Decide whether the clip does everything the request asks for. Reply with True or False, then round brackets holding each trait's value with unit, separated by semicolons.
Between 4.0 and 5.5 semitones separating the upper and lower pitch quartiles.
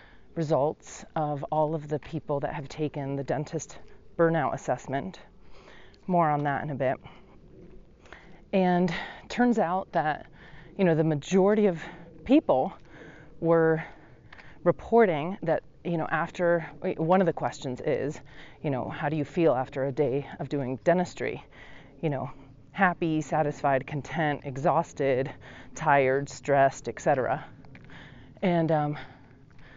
False (3.3 semitones)